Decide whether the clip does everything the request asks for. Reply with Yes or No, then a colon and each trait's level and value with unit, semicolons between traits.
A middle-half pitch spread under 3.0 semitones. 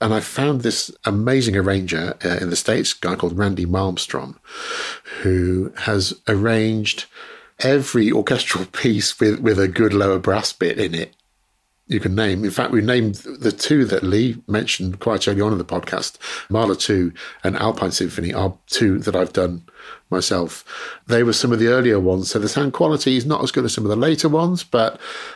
No: average, 4.1 semitones